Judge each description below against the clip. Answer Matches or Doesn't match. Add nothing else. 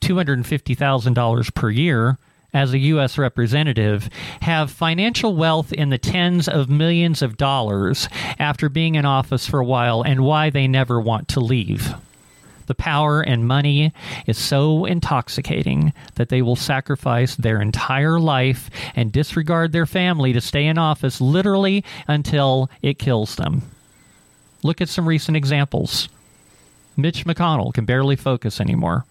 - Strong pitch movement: Doesn't match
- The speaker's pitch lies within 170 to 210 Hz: Doesn't match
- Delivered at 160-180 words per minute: Doesn't match